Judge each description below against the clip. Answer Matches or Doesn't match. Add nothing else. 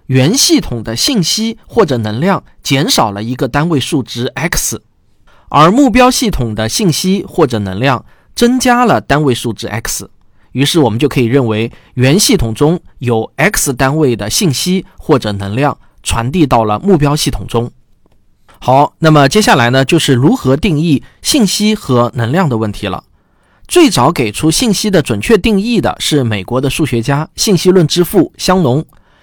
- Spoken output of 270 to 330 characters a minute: Doesn't match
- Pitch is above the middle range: Doesn't match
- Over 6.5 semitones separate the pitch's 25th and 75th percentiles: Matches